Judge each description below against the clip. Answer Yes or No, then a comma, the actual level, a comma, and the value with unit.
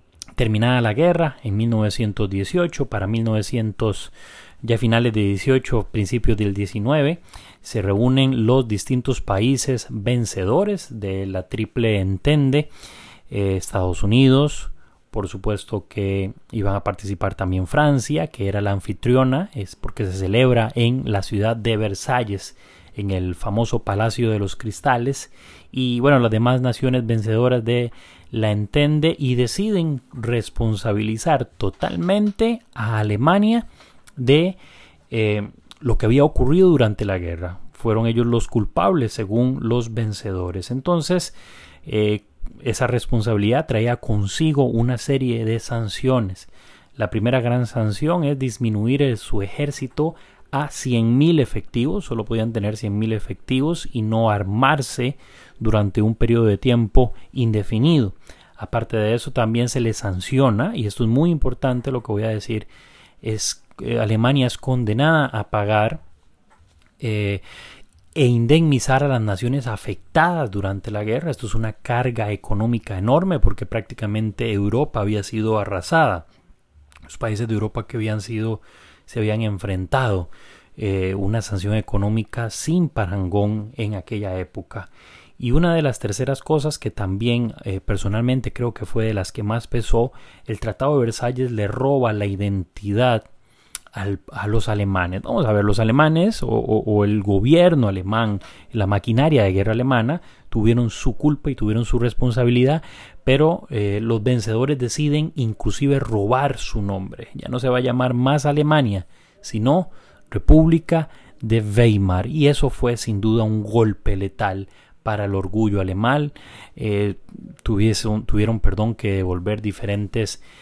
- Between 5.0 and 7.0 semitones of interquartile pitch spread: No, average, 3.9 semitones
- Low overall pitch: Yes, low, 115 Hz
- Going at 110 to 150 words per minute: Yes, average, 140 wpm